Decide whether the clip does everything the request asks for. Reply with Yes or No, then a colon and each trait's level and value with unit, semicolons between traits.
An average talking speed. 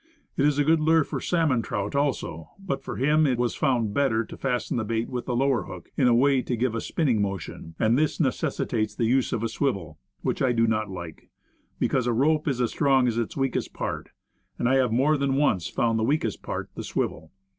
No: fast, 235 wpm